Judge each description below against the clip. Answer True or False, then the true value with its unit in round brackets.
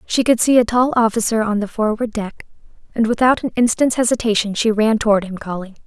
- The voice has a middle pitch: False (220 Hz)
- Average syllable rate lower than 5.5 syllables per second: False (5.8 syllables/s)